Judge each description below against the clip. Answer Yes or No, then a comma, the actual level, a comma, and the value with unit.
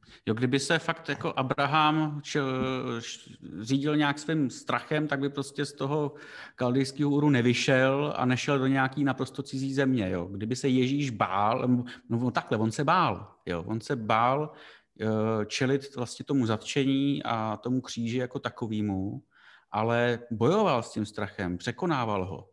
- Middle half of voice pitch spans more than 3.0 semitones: Yes, average, 3.5 semitones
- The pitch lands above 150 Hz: No, low, 130 Hz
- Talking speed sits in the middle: Yes, average, 155 wpm